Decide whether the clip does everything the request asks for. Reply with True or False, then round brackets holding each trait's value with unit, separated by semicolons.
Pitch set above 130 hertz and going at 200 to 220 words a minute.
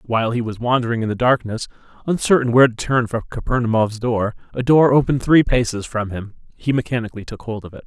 False (120 Hz; 205 wpm)